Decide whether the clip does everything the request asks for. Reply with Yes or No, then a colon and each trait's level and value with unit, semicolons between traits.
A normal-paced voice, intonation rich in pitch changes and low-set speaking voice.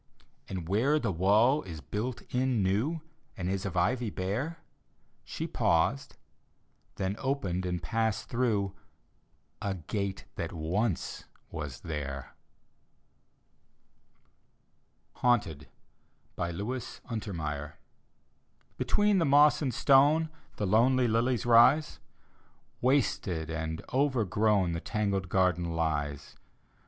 No: slow, 105 wpm; wide, 6.6 semitones; low, 105 Hz